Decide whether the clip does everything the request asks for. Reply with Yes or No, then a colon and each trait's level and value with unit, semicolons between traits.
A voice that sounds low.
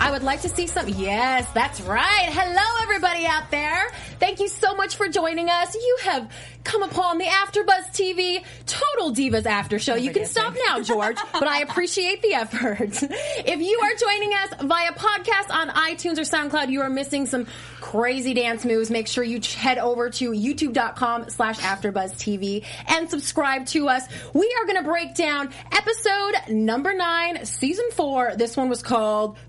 No: very high, 315 Hz